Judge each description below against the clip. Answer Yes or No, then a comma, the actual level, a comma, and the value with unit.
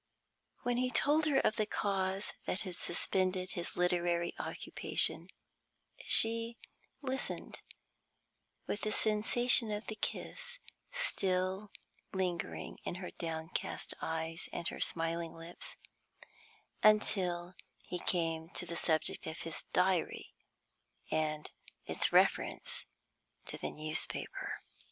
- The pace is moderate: No, slow, 110 wpm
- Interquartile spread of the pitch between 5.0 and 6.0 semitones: No, average, 4.1 semitones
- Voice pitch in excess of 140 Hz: Yes, medium, 185 Hz